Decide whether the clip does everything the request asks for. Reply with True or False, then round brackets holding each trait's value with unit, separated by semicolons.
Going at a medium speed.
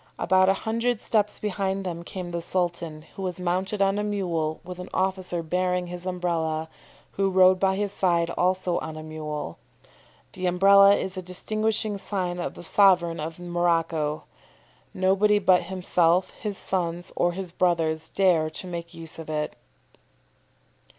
True (155 wpm)